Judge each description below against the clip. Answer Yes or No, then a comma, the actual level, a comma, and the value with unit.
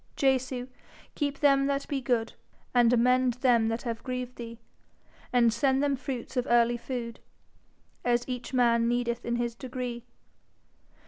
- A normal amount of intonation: No, narrow, 1.6 semitones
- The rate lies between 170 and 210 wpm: No, average, 145 wpm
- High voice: Yes, high, 245 Hz